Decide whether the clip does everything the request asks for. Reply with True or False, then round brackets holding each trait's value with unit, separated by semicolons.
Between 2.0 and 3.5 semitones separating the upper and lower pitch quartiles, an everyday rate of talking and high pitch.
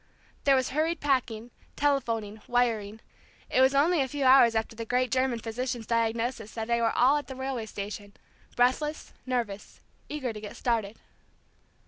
True (2.9 semitones; 160 wpm; 245 Hz)